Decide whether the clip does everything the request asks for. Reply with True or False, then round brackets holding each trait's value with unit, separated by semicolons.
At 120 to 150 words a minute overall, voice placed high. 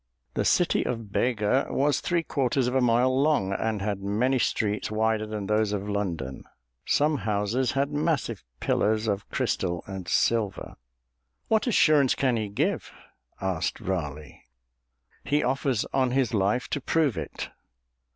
False (145 wpm; 110 Hz)